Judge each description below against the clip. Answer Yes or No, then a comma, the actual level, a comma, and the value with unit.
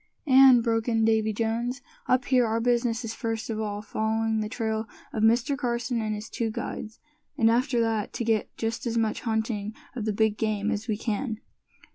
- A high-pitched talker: Yes, high, 225 Hz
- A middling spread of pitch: No, narrow, 1.5 semitones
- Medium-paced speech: Yes, average, 195 wpm